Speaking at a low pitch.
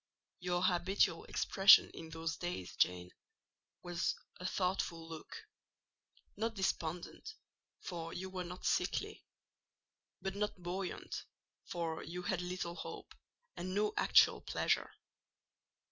No: medium, 180 Hz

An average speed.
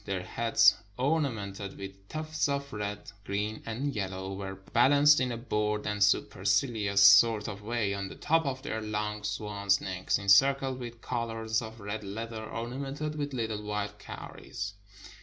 Yes: average, 160 wpm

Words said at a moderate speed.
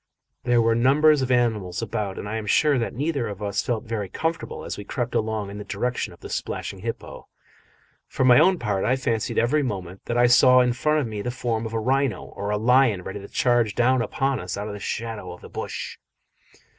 No: fast, 230 wpm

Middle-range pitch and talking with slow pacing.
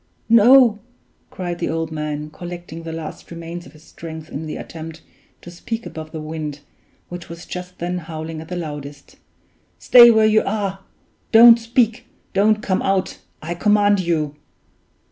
No: medium, 175 Hz; average, 160 wpm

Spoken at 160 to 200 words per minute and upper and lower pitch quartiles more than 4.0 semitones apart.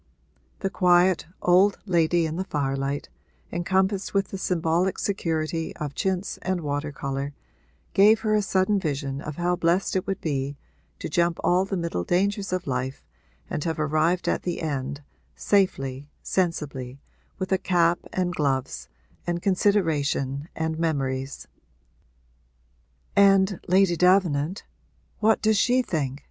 No: slow, 135 wpm; average, 4.7 semitones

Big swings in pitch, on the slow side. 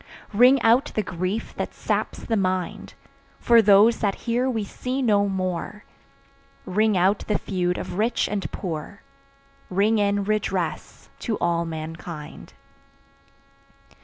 No: average, 3.4 semitones; slow, 130 wpm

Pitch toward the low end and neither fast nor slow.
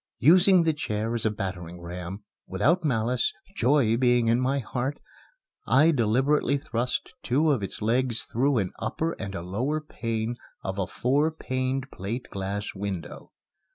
Yes: low, 120 Hz; average, 155 wpm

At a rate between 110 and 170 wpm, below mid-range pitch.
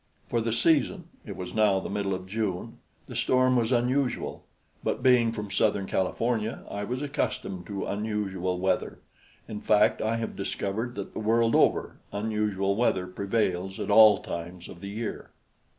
Yes: average, 165 wpm; low, 105 Hz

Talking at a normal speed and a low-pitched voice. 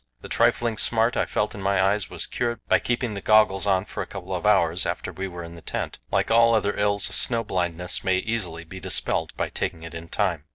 No: fast, 235 wpm; very low, 95 Hz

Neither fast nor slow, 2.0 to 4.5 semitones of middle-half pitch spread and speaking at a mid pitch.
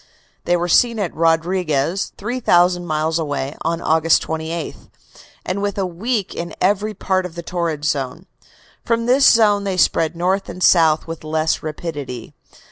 Yes: average, 155 wpm; average, 3.4 semitones; medium, 170 Hz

